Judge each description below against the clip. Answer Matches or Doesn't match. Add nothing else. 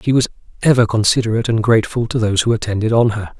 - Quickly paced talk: Matches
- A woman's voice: Doesn't match